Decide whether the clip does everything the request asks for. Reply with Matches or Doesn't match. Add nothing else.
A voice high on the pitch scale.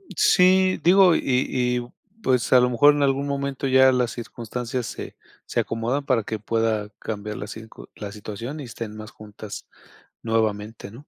Doesn't match